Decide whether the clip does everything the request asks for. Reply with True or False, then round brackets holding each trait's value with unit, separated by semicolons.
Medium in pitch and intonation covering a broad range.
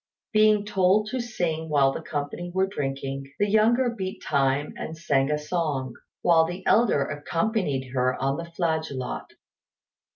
True (160 Hz; 6.0 semitones)